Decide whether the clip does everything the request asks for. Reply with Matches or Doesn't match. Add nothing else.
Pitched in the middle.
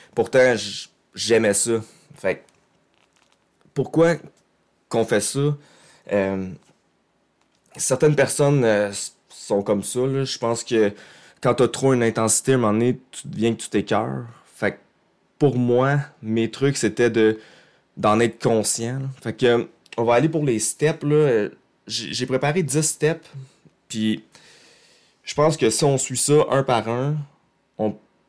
Doesn't match